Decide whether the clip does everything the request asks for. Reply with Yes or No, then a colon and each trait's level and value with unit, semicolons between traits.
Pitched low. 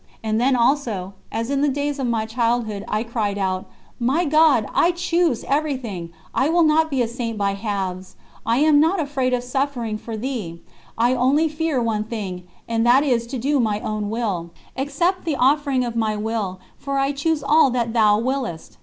No: high, 245 Hz